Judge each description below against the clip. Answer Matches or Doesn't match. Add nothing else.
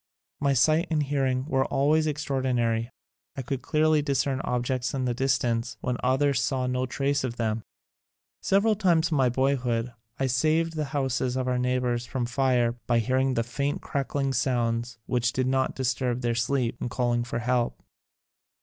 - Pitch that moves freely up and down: Doesn't match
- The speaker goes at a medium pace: Matches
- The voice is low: Matches